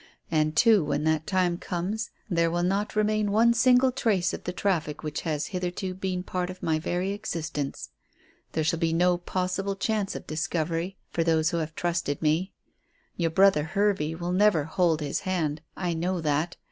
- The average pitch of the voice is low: No, medium, 175 Hz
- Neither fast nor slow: Yes, average, 180 wpm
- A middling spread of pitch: Yes, average, 3.4 semitones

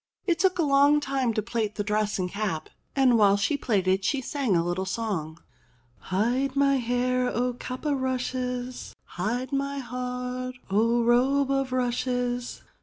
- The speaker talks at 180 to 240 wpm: No, average, 160 wpm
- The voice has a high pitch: Yes, very high, 250 Hz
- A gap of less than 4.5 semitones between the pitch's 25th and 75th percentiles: Yes, average, 3.8 semitones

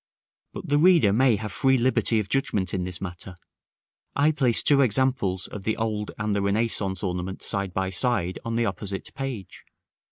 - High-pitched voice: No, low, 105 Hz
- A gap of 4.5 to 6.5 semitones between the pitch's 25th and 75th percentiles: Yes, average, 5.2 semitones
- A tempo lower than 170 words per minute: No, average, 185 wpm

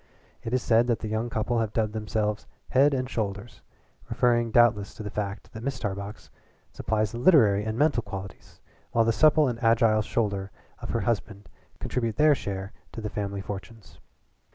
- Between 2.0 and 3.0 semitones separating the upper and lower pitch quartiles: Yes, narrow, 2.4 semitones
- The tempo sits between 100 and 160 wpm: No, average, 175 wpm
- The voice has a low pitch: Yes, low, 110 Hz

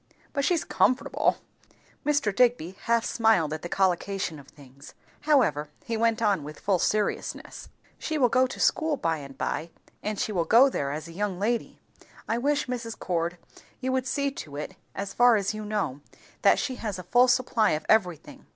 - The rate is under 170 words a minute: No, average, 190 wpm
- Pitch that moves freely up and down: Yes, wide, 6.7 semitones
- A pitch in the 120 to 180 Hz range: No, high, 215 Hz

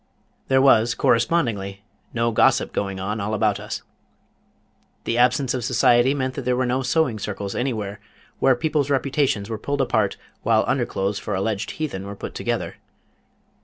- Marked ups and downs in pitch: No, average, 4.5 semitones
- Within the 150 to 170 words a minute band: Yes, average, 165 wpm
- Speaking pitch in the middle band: No, low, 120 Hz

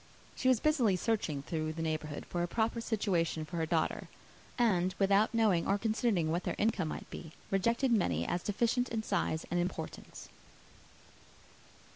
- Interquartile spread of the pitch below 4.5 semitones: No, wide, 5.4 semitones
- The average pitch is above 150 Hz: Yes, high, 190 Hz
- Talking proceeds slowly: No, average, 160 wpm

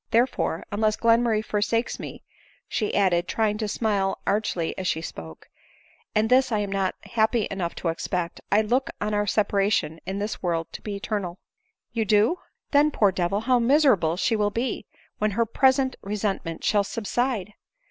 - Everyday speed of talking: Yes, average, 170 wpm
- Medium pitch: No, high, 210 Hz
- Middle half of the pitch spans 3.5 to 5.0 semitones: No, average, 3.0 semitones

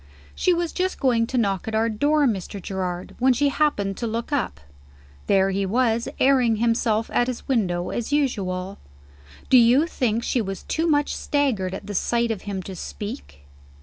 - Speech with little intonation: No, average, 5.1 semitones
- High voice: Yes, high, 230 Hz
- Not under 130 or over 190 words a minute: Yes, average, 180 wpm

